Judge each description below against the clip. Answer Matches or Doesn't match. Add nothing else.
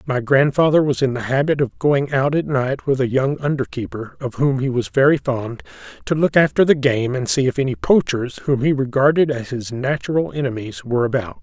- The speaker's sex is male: Matches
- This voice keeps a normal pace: Doesn't match